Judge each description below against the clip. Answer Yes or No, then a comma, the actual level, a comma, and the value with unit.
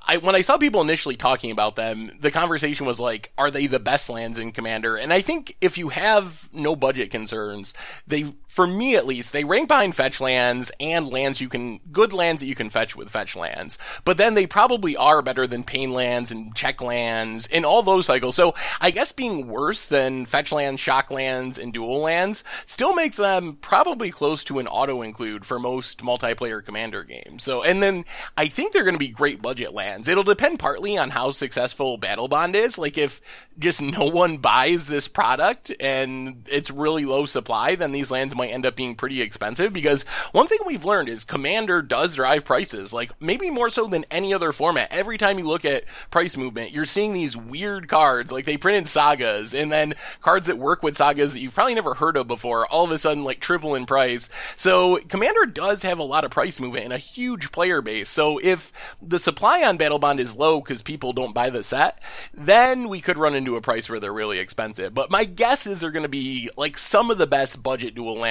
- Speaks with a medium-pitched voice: Yes, medium, 145 Hz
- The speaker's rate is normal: No, fast, 220 wpm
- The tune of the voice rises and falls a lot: Yes, wide, 6.1 semitones